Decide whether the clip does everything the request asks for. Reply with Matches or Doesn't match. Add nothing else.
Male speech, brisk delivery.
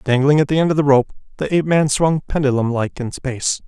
Matches